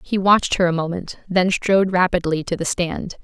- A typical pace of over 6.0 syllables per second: No, 5.4 syllables/s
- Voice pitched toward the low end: No, medium, 180 Hz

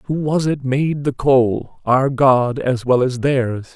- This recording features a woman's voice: No, male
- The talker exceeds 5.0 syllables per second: No, 3.3 syllables/s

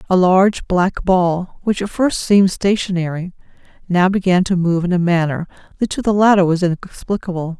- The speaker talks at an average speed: Yes, average, 175 wpm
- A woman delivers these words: Yes, female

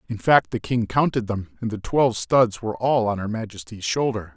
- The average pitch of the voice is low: Yes, low, 110 Hz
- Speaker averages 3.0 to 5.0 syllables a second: No, 5.4 syllables/s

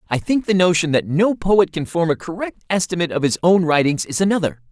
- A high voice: No, medium, 170 Hz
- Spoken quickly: Yes, fast, 230 wpm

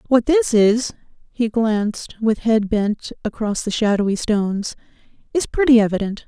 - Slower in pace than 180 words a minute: Yes, slow, 135 wpm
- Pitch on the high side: Yes, high, 220 Hz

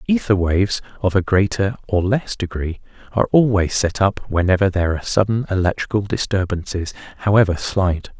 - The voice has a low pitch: Yes, low, 100 Hz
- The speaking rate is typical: Yes, average, 145 wpm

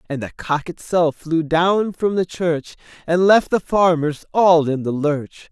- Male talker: Yes, male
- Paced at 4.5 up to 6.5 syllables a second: No, 3.9 syllables/s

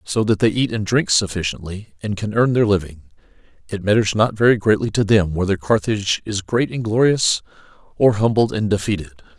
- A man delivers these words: Yes, male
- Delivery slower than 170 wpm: No, average, 185 wpm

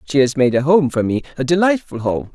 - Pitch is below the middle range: No, medium, 145 Hz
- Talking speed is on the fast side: Yes, fast, 230 wpm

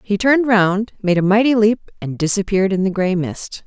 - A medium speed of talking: No, fast, 215 wpm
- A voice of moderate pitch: No, high, 200 Hz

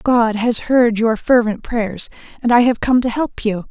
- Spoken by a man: No, female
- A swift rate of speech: Yes, fast, 210 wpm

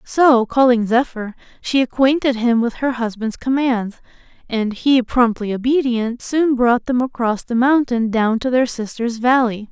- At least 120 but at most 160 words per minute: Yes, average, 155 wpm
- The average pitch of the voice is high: Yes, high, 245 Hz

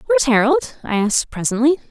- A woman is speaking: Yes, female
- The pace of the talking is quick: No, average, 155 wpm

